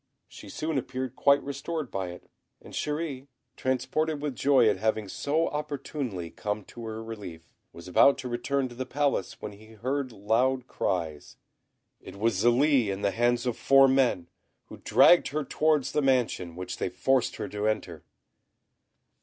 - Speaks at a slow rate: No, average, 165 wpm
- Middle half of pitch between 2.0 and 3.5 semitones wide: No, average, 5.2 semitones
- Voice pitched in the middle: No, low, 125 Hz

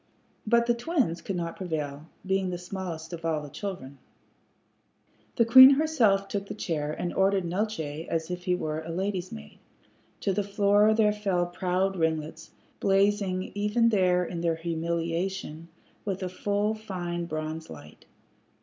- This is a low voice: No, medium, 180 Hz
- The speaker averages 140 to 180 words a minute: Yes, average, 155 wpm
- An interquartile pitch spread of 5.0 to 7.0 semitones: No, average, 3.7 semitones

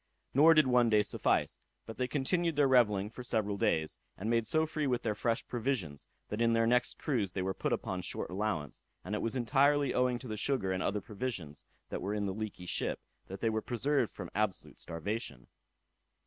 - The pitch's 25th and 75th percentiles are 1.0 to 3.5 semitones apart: No, average, 4.1 semitones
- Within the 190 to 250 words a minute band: Yes, fast, 205 wpm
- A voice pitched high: No, low, 115 Hz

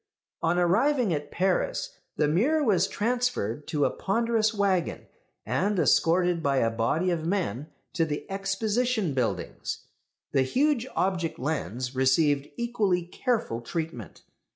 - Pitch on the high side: No, medium, 175 Hz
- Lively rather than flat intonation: Yes, wide, 6.7 semitones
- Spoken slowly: Yes, slow, 130 wpm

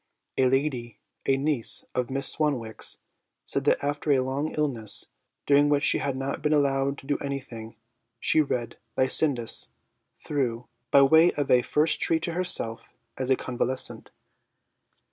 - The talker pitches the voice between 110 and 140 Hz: Yes, low, 135 Hz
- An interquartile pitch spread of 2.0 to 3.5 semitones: Yes, narrow, 2.6 semitones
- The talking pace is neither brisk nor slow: Yes, average, 150 wpm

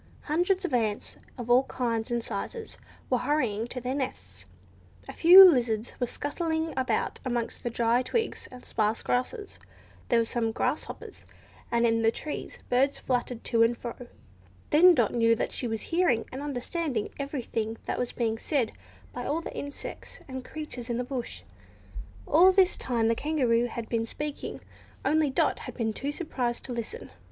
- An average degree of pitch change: Yes, average, 4.2 semitones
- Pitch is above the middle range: Yes, high, 245 Hz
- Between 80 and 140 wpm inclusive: No, average, 170 wpm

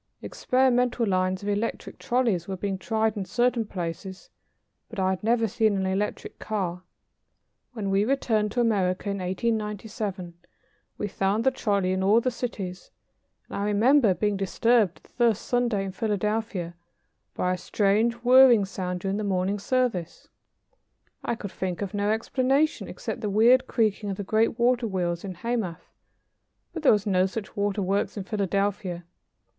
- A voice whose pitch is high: Yes, high, 205 Hz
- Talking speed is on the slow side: No, average, 160 wpm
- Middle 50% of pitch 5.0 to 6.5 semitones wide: No, average, 3.4 semitones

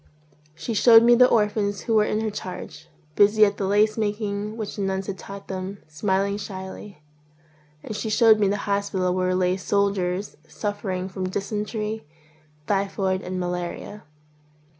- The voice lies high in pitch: Yes, high, 200 Hz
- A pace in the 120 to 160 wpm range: Yes, average, 155 wpm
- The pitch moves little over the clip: Yes, narrow, 2.1 semitones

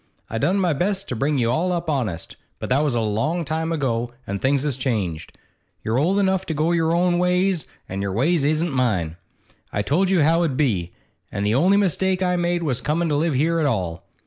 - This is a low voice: No, medium, 150 Hz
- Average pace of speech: No, fast, 225 wpm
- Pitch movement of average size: No, wide, 6.7 semitones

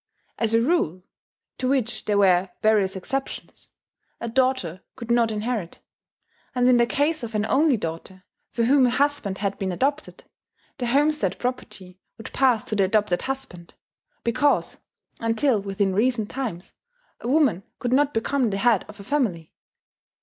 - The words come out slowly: No, average, 155 wpm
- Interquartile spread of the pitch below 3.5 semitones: No, average, 5.0 semitones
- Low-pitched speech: No, high, 230 Hz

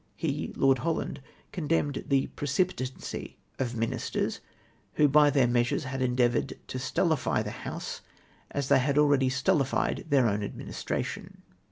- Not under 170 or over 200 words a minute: No, slow, 135 wpm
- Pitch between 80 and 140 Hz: Yes, low, 135 Hz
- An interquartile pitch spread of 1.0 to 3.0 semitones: Yes, narrow, 2.4 semitones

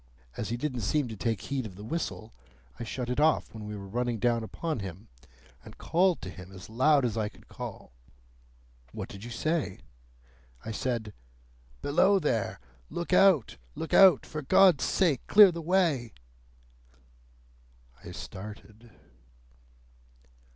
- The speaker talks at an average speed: Yes, average, 150 wpm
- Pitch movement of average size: No, wide, 6.6 semitones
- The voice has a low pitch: Yes, low, 125 Hz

